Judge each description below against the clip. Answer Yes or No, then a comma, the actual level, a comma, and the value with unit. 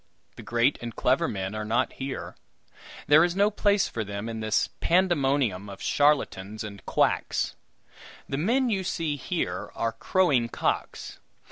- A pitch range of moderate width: No, wide, 7.9 semitones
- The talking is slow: No, average, 150 wpm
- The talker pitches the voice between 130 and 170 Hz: Yes, low, 135 Hz